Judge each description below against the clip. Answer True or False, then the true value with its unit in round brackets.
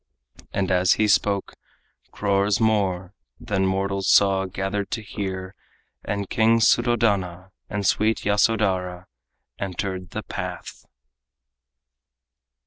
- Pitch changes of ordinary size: False (1.8 semitones)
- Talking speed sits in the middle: False (100 wpm)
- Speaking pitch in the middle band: False (100 Hz)